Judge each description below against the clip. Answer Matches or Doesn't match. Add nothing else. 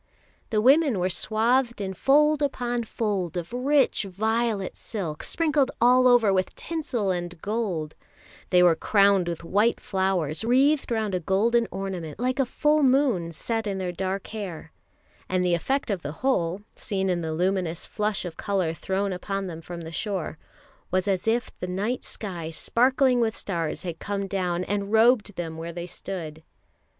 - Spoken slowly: Doesn't match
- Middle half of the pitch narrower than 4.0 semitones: Doesn't match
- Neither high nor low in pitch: Doesn't match